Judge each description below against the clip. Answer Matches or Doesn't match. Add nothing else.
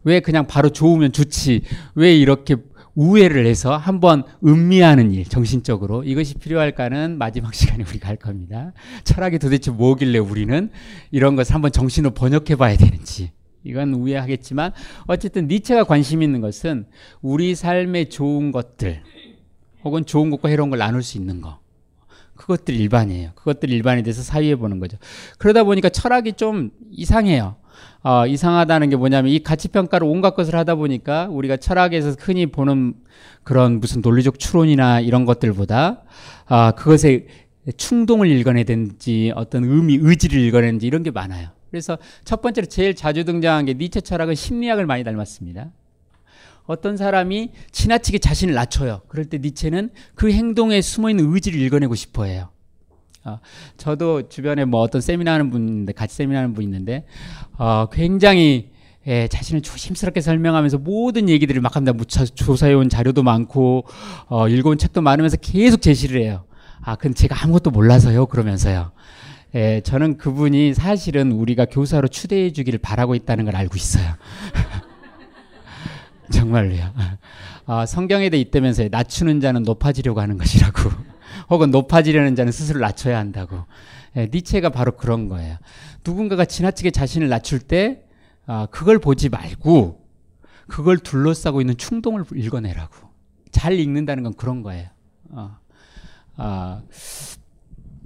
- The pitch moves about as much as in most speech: Doesn't match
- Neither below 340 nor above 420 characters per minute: Matches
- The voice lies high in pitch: Doesn't match